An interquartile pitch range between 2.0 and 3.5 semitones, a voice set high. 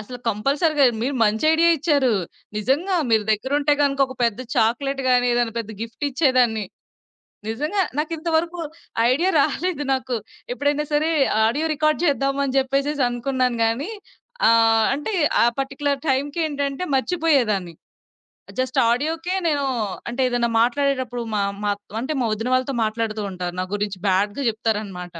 No: average, 4.4 semitones; very high, 265 Hz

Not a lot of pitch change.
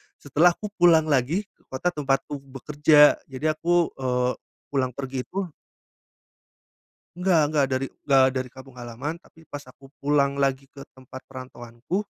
No: average, 3.3 semitones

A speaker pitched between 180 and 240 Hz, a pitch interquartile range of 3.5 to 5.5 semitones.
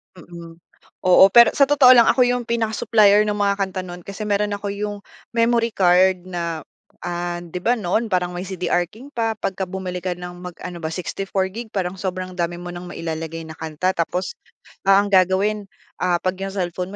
No: medium, 185 Hz; average, 2.8 semitones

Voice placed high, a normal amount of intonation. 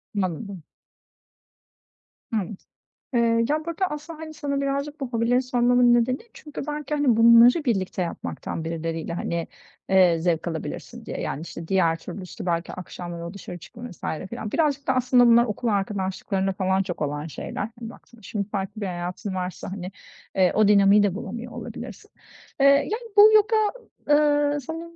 No: high, 225 Hz; wide, 7.1 semitones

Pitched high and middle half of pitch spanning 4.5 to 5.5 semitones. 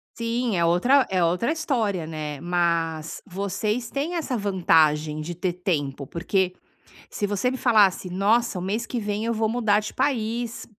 Yes: high, 200 Hz; average, 5.2 semitones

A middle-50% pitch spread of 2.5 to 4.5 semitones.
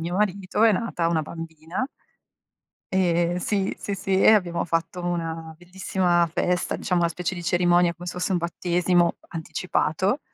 No: narrow, 1.7 semitones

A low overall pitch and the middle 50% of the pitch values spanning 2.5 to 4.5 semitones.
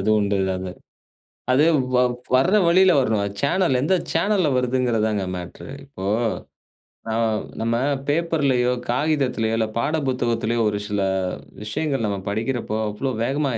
No: low, 125 Hz; average, 4.9 semitones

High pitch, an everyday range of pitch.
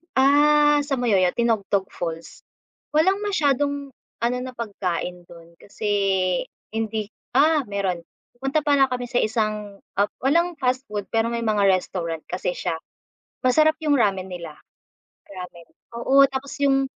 No: high, 235 Hz; wide, 6.3 semitones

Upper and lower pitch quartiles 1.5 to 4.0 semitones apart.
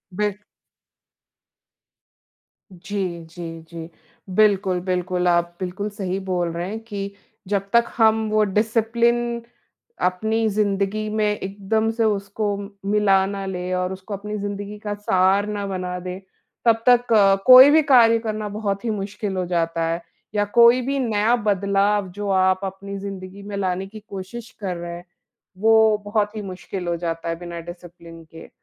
Yes: average, 2.7 semitones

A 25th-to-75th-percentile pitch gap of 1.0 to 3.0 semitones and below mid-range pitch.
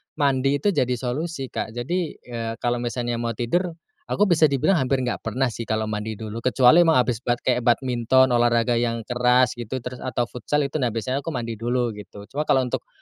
Yes: narrow, 2.5 semitones; low, 125 Hz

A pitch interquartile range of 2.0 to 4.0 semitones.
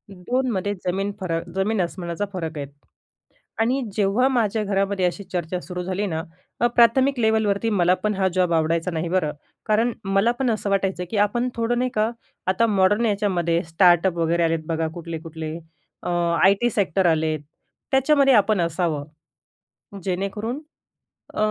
No: average, 4.4 semitones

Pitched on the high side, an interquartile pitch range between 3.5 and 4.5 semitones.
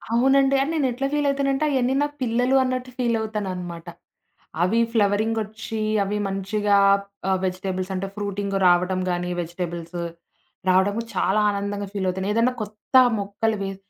Yes: high, 205 Hz; average, 3.9 semitones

